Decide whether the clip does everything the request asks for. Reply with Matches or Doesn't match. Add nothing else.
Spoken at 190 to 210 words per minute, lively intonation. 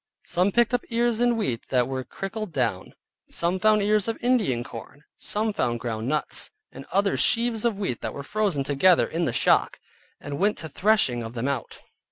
Matches